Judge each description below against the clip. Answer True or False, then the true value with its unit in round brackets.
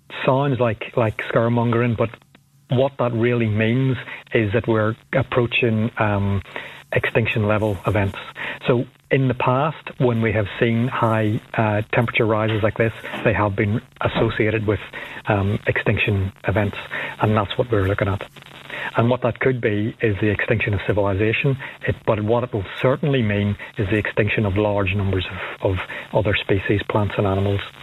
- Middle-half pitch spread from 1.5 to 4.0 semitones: True (2.7 semitones)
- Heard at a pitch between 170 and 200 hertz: False (115 Hz)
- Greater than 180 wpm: False (160 wpm)